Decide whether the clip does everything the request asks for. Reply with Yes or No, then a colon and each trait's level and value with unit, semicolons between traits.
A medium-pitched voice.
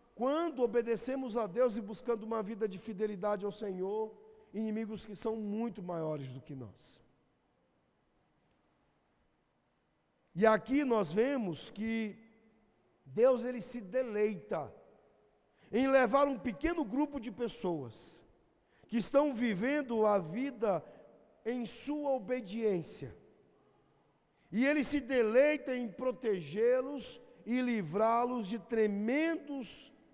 No: high, 230 Hz